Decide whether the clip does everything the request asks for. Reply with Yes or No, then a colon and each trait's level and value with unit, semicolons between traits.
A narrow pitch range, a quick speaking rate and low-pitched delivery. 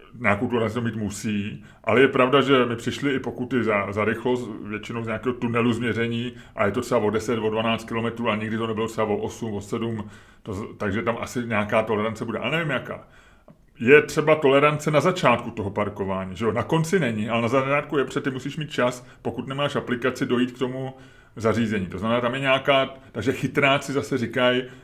No: average, 3.2 semitones; fast, 210 wpm; low, 120 Hz